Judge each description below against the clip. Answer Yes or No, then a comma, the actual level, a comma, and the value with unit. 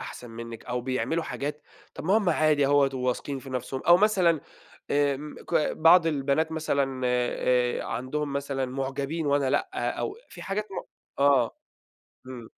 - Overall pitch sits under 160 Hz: Yes, medium, 140 Hz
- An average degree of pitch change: Yes, average, 3.6 semitones